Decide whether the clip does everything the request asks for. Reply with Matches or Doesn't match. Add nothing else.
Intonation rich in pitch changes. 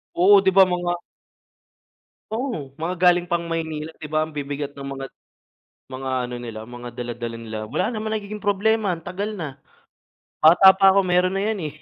Matches